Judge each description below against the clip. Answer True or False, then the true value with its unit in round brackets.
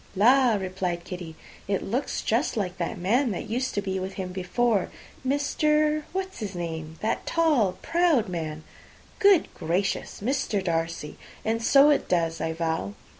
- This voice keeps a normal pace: True (155 wpm)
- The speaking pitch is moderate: False (200 Hz)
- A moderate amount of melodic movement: False (7.2 semitones)